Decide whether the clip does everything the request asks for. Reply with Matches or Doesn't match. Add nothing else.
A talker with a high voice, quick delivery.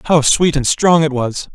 Doesn't match